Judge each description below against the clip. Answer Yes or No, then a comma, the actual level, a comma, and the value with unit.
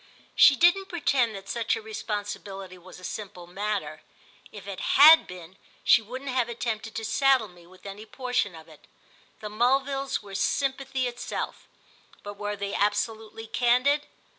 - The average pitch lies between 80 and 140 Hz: No, high, 220 Hz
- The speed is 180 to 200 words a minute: No, average, 155 wpm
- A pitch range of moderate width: Yes, average, 4.6 semitones